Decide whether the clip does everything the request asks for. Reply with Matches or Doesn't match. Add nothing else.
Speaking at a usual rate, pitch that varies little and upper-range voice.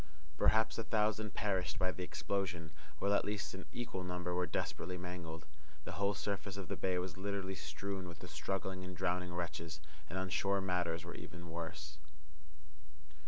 Doesn't match